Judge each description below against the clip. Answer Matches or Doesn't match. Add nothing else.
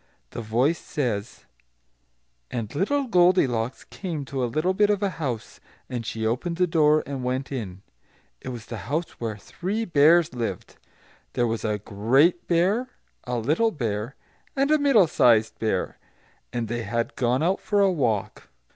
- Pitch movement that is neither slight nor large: Doesn't match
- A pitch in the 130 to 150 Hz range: Matches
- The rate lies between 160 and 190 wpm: Matches